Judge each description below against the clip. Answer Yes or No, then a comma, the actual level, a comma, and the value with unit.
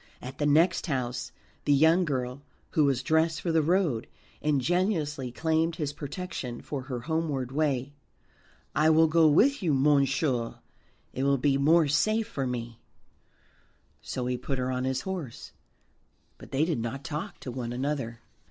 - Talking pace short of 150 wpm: No, average, 160 wpm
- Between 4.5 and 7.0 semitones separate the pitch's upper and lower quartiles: No, average, 3.8 semitones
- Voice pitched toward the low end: No, medium, 145 Hz